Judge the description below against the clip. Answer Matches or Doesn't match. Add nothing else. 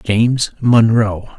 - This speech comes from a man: Matches